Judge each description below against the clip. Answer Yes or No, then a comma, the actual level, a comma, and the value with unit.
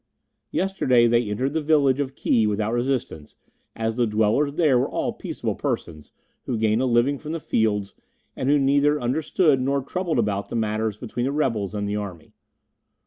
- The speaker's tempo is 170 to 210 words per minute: Yes, average, 180 wpm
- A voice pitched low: Yes, low, 120 Hz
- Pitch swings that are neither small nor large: Yes, average, 4.7 semitones